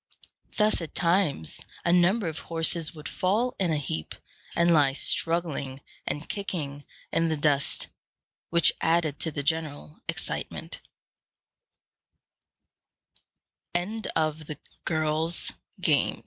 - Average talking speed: No, slow, 95 wpm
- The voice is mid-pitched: Yes, medium, 165 Hz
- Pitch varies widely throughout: No, average, 3.0 semitones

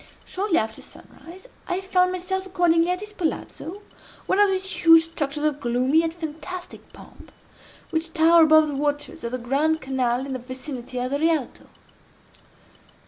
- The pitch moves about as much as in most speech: Yes, average, 4.7 semitones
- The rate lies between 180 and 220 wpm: No, average, 160 wpm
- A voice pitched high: Yes, very high, 320 Hz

